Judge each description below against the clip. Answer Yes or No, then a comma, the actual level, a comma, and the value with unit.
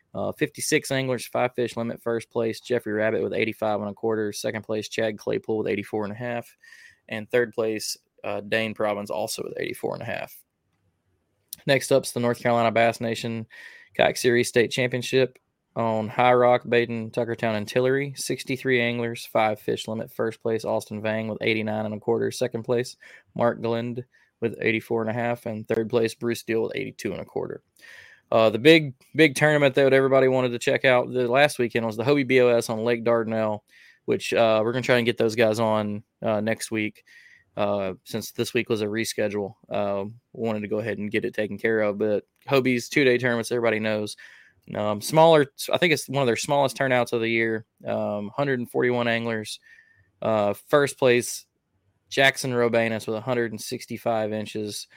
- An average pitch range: No, narrow, 2.3 semitones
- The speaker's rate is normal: Yes, average, 185 wpm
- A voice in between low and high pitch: No, low, 115 Hz